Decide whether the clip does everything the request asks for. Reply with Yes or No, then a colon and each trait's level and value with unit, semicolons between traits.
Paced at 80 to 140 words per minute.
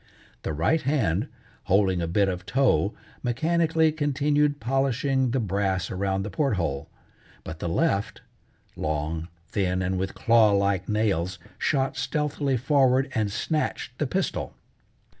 Yes: slow, 135 wpm